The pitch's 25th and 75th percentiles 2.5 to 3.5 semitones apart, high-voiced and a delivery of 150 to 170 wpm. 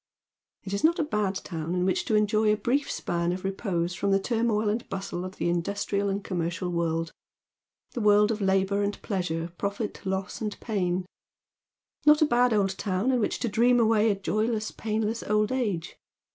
No: average, 2.9 semitones; high, 205 Hz; average, 195 wpm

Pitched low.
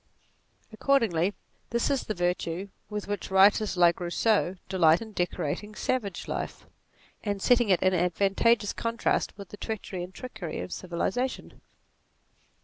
No: high, 200 Hz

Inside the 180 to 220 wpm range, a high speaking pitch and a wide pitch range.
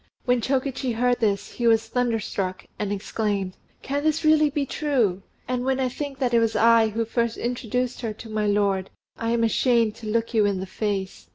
No: average, 200 wpm; high, 230 Hz; average, 3.1 semitones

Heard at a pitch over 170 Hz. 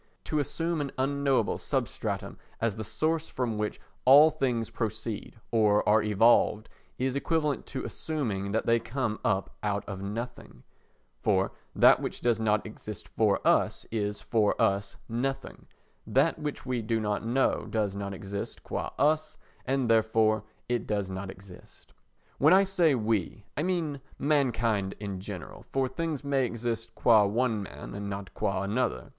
No: low, 115 Hz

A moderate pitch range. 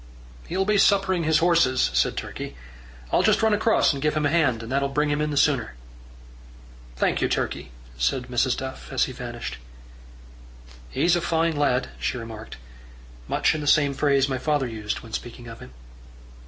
Yes: average, 4.5 semitones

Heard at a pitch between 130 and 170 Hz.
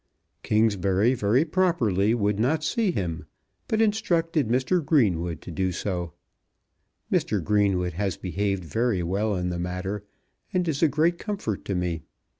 No: low, 105 Hz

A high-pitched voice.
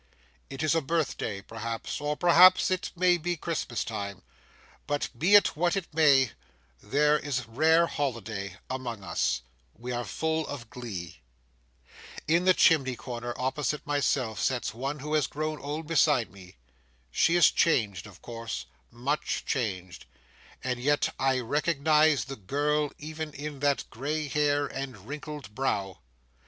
No: medium, 140 Hz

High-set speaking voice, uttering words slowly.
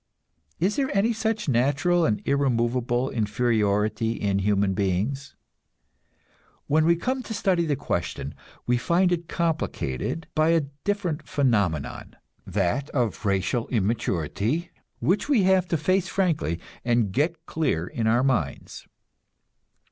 No: low, 135 Hz; slow, 125 wpm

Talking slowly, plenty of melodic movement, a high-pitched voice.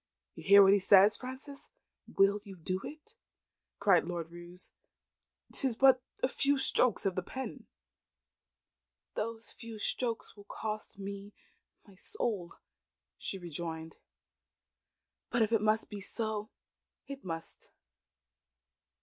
No: slow, 125 wpm; average, 3.8 semitones; high, 205 Hz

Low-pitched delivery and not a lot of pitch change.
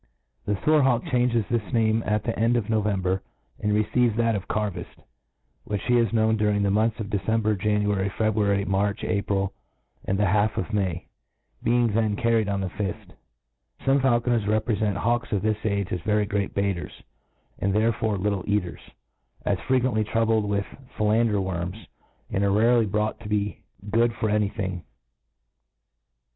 Yes: low, 105 Hz; narrow, 2.1 semitones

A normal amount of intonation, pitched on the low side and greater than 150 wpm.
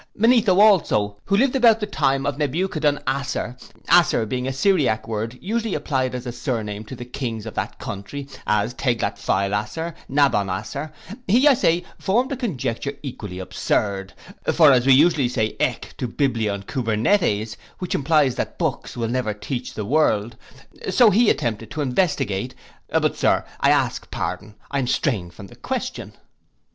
No: wide, 7.0 semitones; low, 130 Hz; average, 165 wpm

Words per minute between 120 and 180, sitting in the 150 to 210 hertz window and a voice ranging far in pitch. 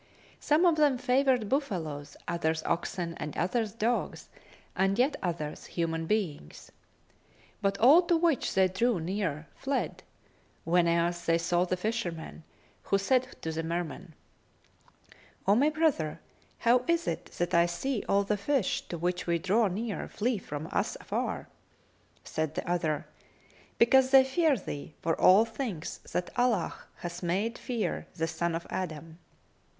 Yes: average, 145 wpm; high, 190 Hz; wide, 6.5 semitones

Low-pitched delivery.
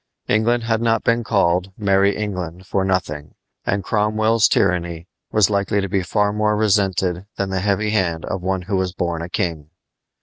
Yes: very low, 95 Hz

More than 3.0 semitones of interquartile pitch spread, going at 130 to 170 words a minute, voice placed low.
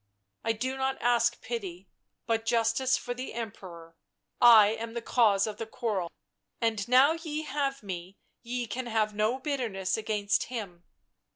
No: average, 3.5 semitones; average, 160 wpm; high, 225 Hz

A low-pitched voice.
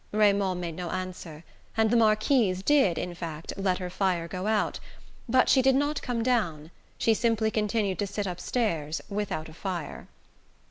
No: high, 200 Hz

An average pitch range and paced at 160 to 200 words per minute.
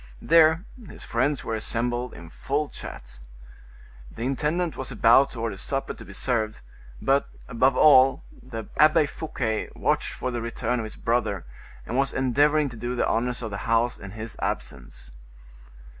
Yes: average, 3.5 semitones; average, 165 wpm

